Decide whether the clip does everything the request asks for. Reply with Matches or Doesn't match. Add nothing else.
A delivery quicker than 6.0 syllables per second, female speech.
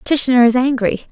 Doesn't match